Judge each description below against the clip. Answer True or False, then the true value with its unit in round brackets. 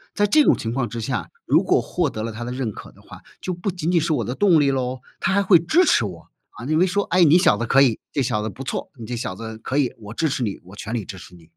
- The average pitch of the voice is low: True (130 Hz)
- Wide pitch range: True (7.2 semitones)